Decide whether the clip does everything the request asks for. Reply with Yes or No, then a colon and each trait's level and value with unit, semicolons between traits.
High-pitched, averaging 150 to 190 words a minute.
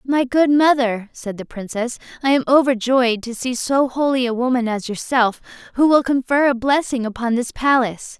Yes: very high, 250 Hz; average, 185 wpm